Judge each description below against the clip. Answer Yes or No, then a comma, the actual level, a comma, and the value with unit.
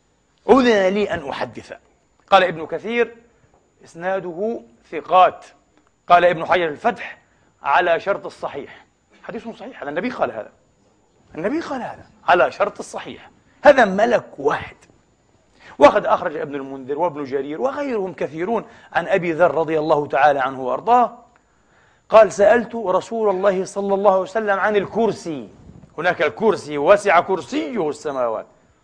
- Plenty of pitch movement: No, average, 4.9 semitones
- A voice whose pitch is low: No, high, 190 Hz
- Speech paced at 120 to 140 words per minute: Yes, average, 125 wpm